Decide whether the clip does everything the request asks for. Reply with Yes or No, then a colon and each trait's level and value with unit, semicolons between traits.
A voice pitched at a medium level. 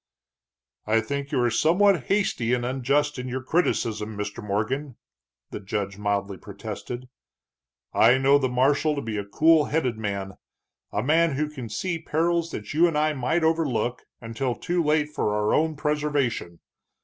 No: low, 130 Hz